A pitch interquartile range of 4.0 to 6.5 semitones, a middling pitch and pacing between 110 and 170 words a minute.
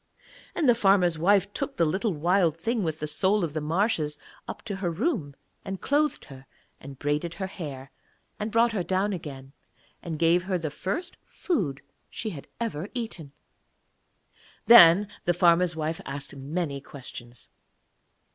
Yes: average, 5.3 semitones; medium, 175 Hz; average, 160 wpm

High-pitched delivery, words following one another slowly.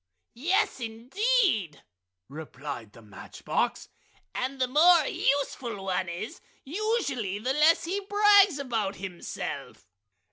Yes: very high, 255 Hz; slow, 110 wpm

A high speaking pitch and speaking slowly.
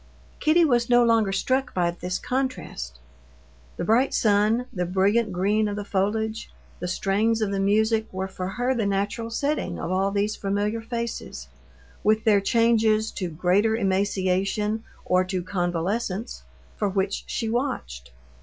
No: high, 205 Hz; average, 150 wpm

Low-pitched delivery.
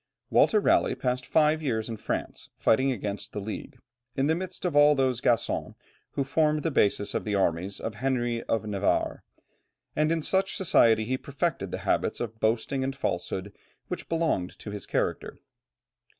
Yes: low, 125 Hz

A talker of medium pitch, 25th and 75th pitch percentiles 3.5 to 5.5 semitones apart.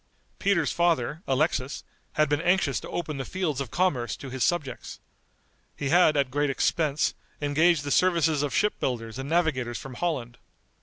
Yes: medium, 145 Hz; average, 4.2 semitones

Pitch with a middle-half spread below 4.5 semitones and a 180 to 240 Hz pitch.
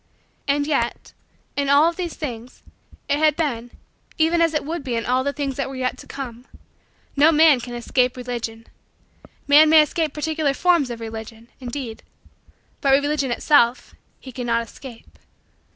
No: average, 3.9 semitones; very high, 275 Hz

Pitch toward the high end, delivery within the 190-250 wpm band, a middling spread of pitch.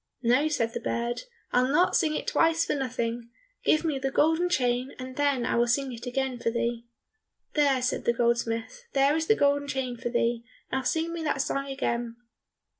Yes: very high, 260 Hz; average, 195 wpm; average, 3.4 semitones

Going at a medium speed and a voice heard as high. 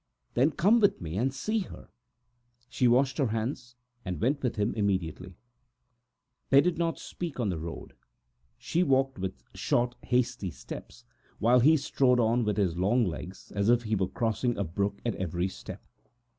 No: average, 170 wpm; low, 120 Hz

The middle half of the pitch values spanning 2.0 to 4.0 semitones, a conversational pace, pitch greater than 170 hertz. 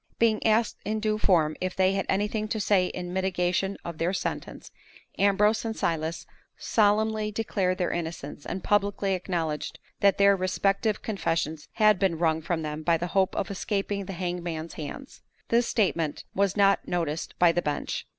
Yes: average, 3.4 semitones; average, 170 wpm; high, 190 Hz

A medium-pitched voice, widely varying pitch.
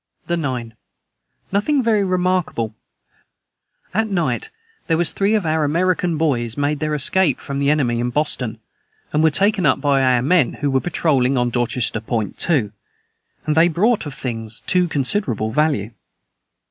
Yes: medium, 150 Hz; wide, 6.2 semitones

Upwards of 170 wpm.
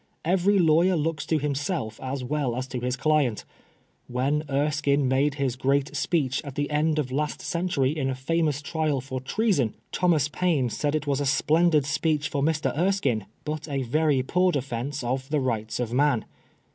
Yes: average, 180 wpm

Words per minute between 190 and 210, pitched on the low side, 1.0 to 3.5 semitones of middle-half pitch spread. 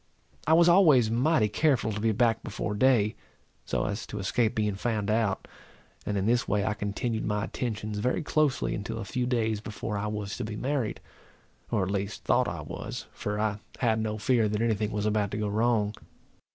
Yes: fast, 205 wpm; low, 110 Hz; narrow, 2.5 semitones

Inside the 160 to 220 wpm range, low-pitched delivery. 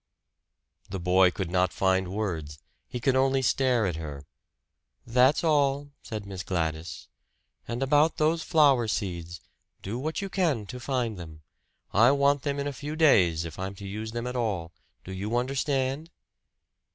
Yes: average, 165 wpm; low, 115 Hz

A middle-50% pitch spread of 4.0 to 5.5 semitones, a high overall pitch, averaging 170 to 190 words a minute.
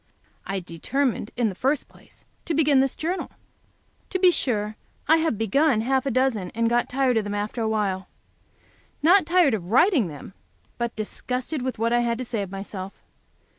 Yes: average, 4.8 semitones; high, 240 Hz; average, 185 wpm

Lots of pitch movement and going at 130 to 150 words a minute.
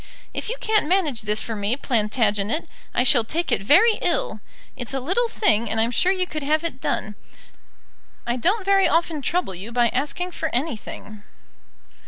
No: wide, 7.9 semitones; average, 180 wpm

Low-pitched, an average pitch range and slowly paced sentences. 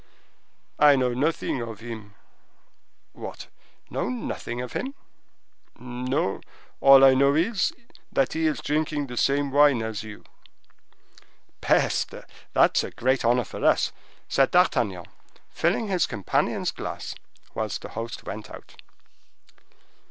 Yes: low, 130 Hz; average, 4.0 semitones; slow, 120 wpm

